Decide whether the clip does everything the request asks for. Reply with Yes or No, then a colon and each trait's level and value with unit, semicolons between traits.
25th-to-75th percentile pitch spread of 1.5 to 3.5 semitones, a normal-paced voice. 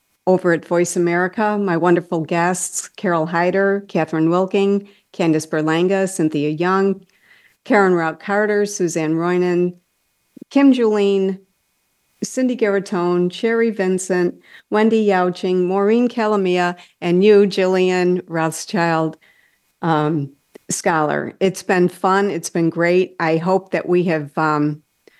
No: average, 2.7 semitones; slow, 115 wpm